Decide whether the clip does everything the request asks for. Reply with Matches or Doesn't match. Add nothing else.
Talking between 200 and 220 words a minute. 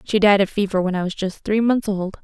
Doesn't match